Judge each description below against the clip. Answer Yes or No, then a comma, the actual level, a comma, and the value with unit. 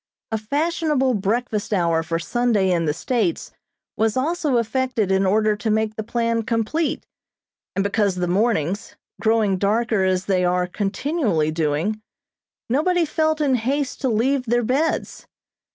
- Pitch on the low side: No, high, 220 Hz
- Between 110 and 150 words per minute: Yes, average, 145 wpm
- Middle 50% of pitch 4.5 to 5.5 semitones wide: Yes, average, 5.2 semitones